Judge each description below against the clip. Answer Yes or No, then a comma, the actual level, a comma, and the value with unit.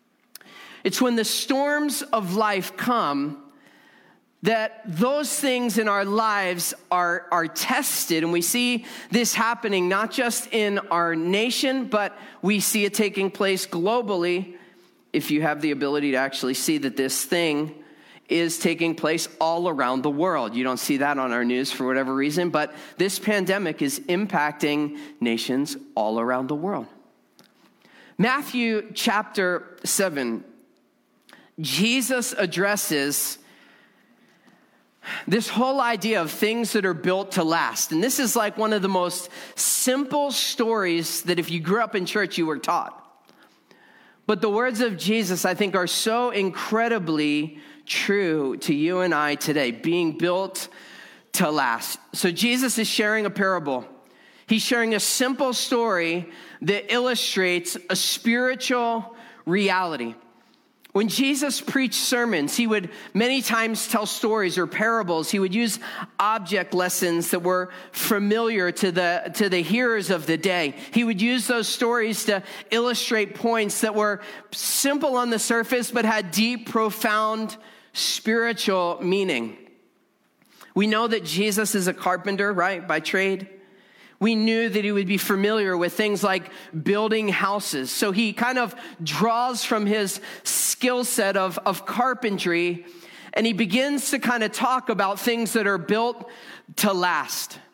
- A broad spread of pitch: No, average, 4.7 semitones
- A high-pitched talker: Yes, high, 200 Hz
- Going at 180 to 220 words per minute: No, average, 145 wpm